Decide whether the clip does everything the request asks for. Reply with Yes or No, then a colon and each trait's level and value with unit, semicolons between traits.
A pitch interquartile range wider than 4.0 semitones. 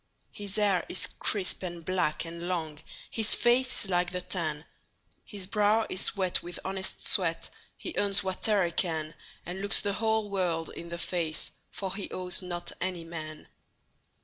No: average, 2.9 semitones